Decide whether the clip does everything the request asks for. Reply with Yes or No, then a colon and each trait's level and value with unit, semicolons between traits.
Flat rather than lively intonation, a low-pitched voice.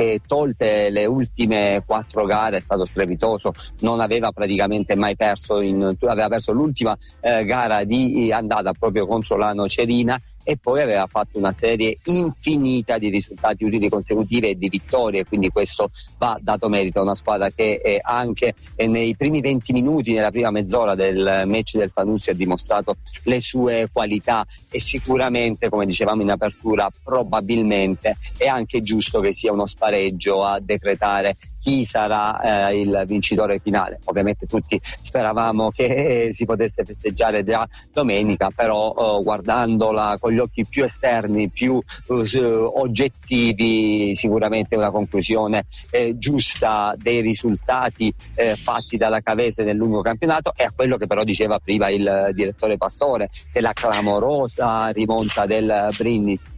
Yes: narrow, 2.3 semitones; low, 110 Hz